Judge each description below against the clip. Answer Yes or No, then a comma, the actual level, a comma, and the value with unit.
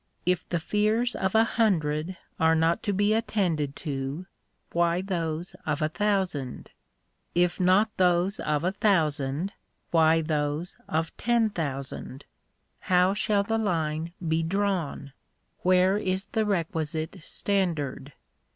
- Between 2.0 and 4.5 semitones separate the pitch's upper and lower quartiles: Yes, average, 4.1 semitones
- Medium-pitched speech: Yes, medium, 175 Hz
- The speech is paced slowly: Yes, slow, 125 wpm